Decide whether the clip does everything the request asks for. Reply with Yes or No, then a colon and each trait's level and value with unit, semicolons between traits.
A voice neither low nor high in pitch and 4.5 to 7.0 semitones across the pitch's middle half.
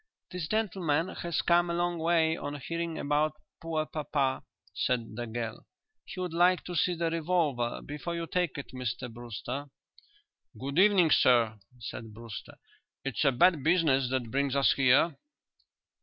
Yes: medium, 150 Hz; average, 5.1 semitones